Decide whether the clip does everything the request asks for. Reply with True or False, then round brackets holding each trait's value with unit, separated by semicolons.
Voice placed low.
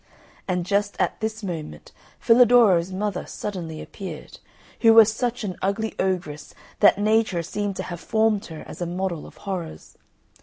False (195 Hz)